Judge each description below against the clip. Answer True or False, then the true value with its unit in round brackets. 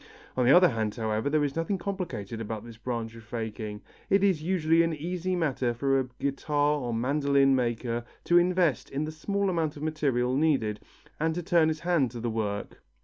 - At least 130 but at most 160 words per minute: False (200 wpm)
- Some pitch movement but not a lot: False (5.9 semitones)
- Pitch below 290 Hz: True (140 Hz)